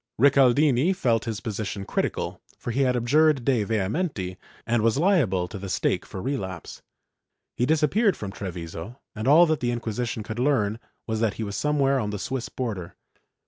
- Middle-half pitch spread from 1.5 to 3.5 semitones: No, average, 5.1 semitones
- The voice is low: Yes, low, 120 Hz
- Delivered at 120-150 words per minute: No, average, 180 wpm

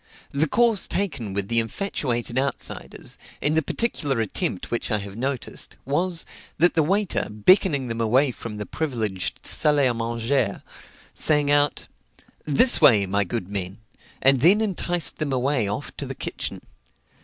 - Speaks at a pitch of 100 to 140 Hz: Yes, low, 135 Hz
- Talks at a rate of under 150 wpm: No, average, 155 wpm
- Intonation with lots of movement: Yes, wide, 5.9 semitones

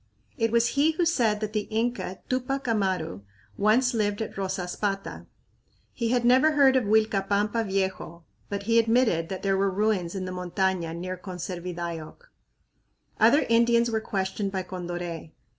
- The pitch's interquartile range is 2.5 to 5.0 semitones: Yes, average, 4.1 semitones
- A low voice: No, high, 205 Hz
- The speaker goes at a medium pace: Yes, average, 150 wpm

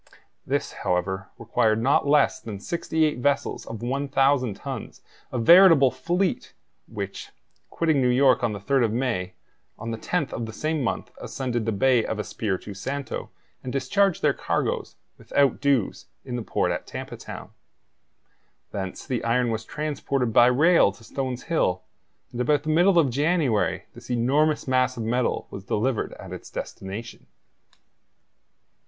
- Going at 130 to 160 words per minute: Yes, average, 155 wpm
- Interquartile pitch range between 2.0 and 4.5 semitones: Yes, average, 4.0 semitones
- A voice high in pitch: No, low, 125 Hz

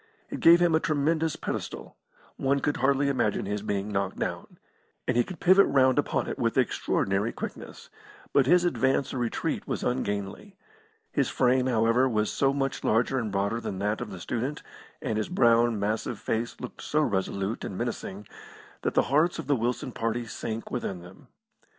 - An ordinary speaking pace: Yes, average, 180 wpm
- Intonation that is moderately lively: Yes, average, 4.7 semitones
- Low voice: Yes, low, 120 Hz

